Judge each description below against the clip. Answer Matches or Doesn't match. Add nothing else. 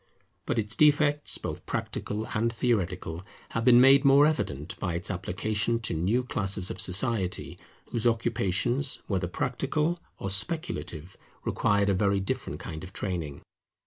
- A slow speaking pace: Doesn't match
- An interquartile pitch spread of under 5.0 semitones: Doesn't match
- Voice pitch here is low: Matches